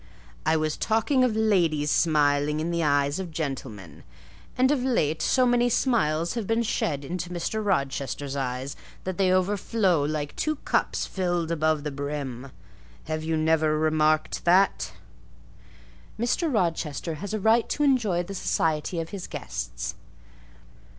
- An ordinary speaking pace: Yes, average, 145 wpm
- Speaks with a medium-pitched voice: Yes, medium, 165 Hz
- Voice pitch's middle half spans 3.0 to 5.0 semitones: No, wide, 5.5 semitones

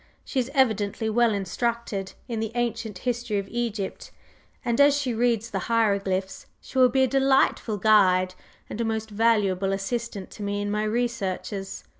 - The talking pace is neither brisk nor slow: Yes, average, 165 wpm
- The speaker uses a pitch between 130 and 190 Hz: No, high, 220 Hz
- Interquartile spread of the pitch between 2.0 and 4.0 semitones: Yes, average, 3.0 semitones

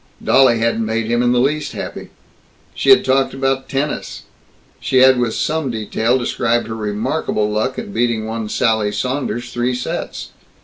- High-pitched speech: No, low, 120 Hz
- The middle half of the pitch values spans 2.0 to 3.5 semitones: Yes, average, 2.8 semitones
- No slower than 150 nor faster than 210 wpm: Yes, average, 165 wpm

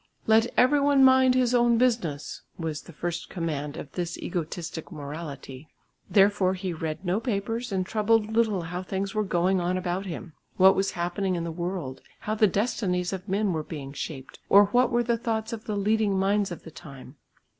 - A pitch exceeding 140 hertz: Yes, high, 190 Hz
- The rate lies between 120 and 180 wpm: No, average, 190 wpm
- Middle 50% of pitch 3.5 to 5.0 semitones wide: Yes, average, 4.5 semitones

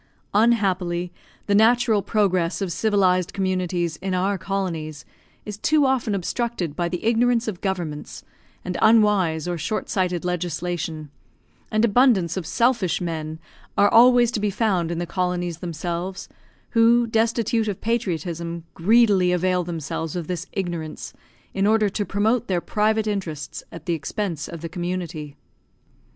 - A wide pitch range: No, average, 4.1 semitones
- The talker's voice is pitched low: No, medium, 185 Hz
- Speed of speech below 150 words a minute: Yes, average, 140 wpm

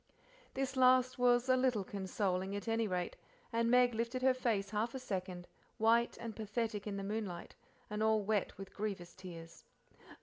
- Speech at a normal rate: Yes, average, 170 wpm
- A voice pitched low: No, high, 220 Hz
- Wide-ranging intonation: No, average, 3.7 semitones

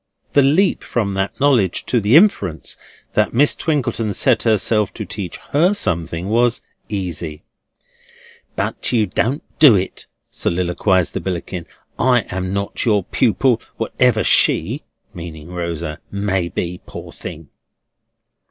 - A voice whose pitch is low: Yes, low, 100 Hz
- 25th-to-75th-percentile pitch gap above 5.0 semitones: Yes, wide, 5.5 semitones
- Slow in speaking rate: Yes, slow, 130 wpm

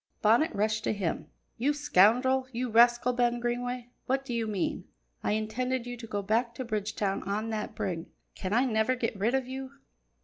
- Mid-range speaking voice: No, high, 235 Hz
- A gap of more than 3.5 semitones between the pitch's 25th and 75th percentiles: No, average, 2.8 semitones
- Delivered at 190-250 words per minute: Yes, average, 195 wpm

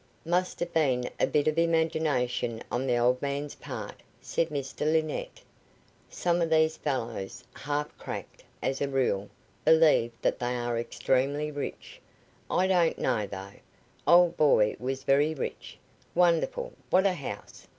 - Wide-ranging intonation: No, average, 4.7 semitones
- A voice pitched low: No, medium, 145 Hz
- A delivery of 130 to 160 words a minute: Yes, average, 150 wpm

